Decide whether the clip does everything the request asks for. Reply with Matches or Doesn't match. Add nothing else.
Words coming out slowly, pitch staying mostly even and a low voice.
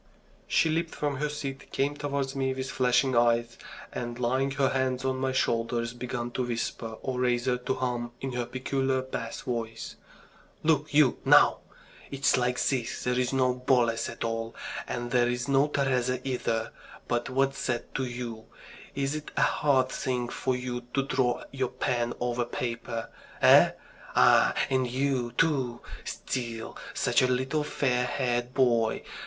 Doesn't match